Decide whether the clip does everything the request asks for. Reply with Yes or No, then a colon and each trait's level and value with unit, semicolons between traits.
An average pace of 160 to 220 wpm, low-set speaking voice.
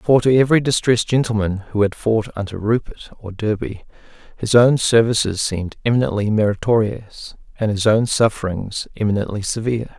No: average, 145 wpm; low, 110 Hz